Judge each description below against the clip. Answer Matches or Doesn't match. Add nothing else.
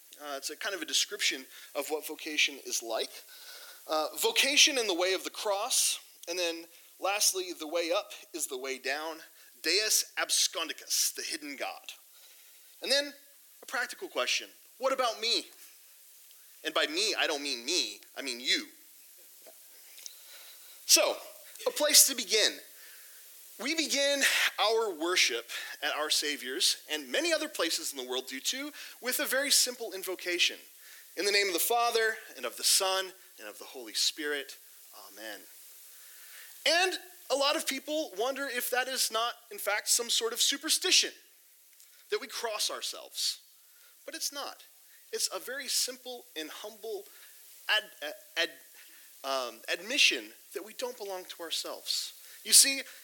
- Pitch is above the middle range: Matches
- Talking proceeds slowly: Doesn't match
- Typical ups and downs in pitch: Doesn't match